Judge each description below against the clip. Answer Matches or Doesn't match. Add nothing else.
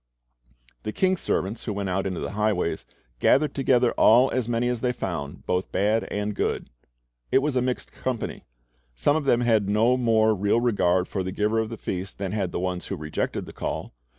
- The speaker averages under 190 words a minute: Doesn't match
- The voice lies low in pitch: Matches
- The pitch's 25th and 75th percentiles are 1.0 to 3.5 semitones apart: Doesn't match